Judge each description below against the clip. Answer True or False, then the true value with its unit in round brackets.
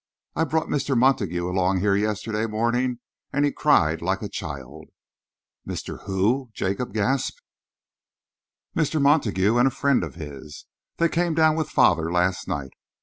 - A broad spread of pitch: True (7.2 semitones)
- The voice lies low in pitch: True (110 Hz)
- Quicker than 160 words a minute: False (145 wpm)